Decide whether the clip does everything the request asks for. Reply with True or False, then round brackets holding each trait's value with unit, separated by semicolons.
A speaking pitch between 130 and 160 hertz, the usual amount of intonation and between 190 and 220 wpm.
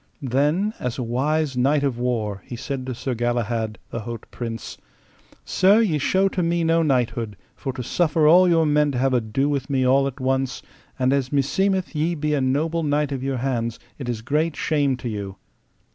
True (135 Hz; 3.9 semitones; 200 wpm)